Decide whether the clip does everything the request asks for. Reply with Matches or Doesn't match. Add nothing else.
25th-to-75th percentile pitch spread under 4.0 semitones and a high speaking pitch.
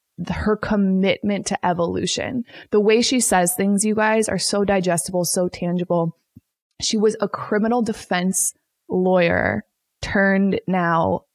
Matches